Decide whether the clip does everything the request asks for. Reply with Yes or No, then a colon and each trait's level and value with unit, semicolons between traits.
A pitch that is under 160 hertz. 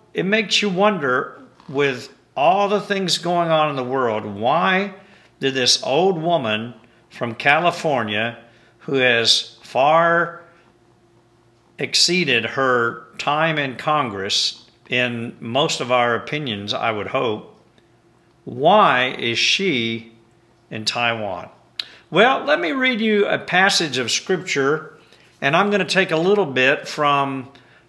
Yes: low, 135 Hz